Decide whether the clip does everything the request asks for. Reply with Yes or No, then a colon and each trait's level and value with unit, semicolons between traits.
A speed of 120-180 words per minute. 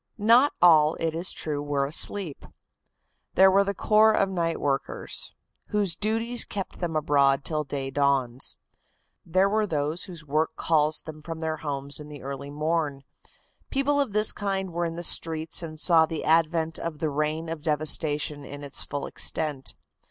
Yes: average, 170 wpm